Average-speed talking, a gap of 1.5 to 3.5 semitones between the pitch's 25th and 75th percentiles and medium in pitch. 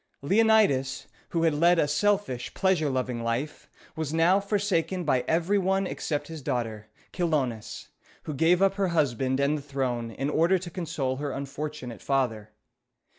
No: average, 165 wpm; average, 5.2 semitones; medium, 150 Hz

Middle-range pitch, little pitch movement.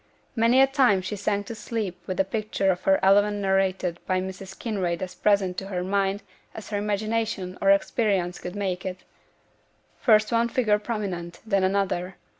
No: high, 195 Hz; narrow, 2.3 semitones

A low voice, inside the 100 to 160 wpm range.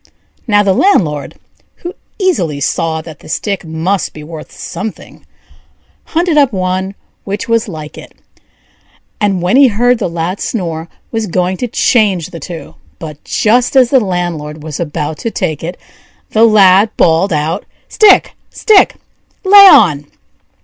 No: medium, 185 Hz; average, 150 wpm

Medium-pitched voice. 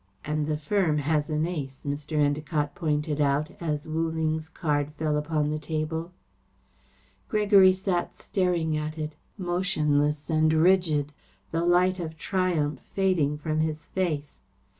Yes: medium, 155 Hz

